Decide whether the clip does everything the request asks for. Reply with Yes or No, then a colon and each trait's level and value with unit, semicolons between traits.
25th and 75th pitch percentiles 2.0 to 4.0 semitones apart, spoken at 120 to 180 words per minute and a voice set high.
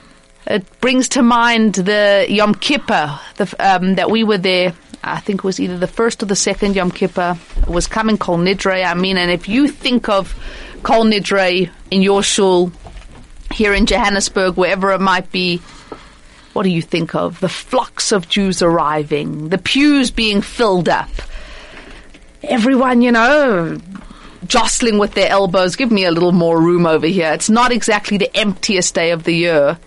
Yes: average, 3.5 semitones; average, 175 wpm; high, 195 Hz